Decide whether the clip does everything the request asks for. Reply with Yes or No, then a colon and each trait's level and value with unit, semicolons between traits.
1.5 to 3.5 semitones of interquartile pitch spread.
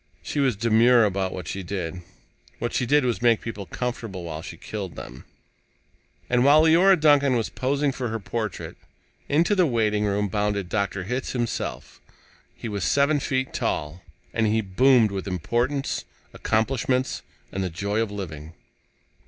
No: average, 4.9 semitones